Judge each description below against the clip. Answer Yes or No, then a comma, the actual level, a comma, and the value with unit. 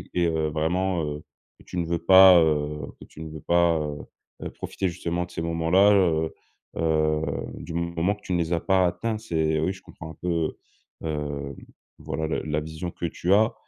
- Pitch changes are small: Yes, narrow, 2.3 semitones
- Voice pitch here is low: Yes, very low, 85 Hz